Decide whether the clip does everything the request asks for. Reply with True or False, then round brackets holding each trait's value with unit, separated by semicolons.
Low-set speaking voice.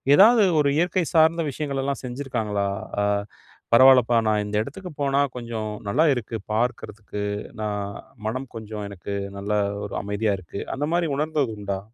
True (120 Hz)